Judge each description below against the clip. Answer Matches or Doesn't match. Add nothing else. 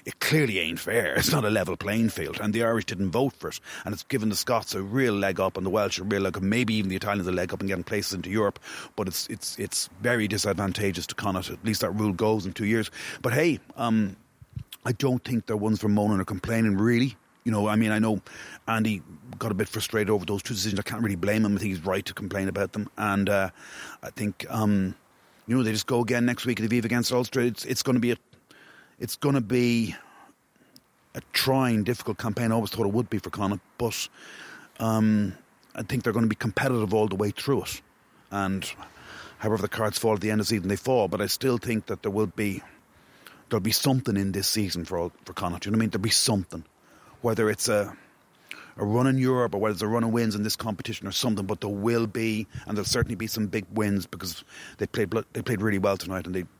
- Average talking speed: Doesn't match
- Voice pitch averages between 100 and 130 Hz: Matches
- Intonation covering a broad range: Doesn't match